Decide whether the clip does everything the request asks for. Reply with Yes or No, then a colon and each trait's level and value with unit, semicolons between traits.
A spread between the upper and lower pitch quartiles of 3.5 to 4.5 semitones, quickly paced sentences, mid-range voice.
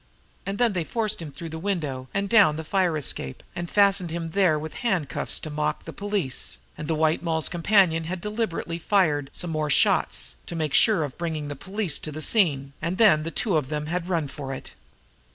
Yes: average, 4.1 semitones; fast, 210 wpm; medium, 165 Hz